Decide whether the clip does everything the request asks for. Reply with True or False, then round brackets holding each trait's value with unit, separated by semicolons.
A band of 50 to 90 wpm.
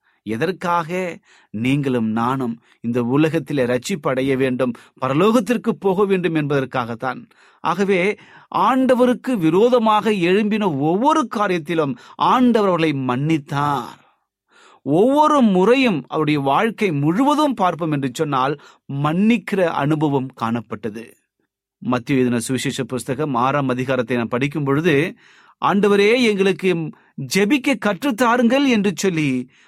True (85 wpm)